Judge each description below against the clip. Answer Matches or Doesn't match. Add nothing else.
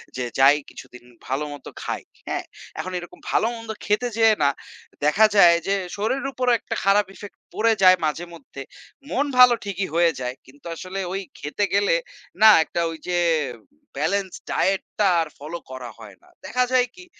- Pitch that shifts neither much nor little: Doesn't match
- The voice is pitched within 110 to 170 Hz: Doesn't match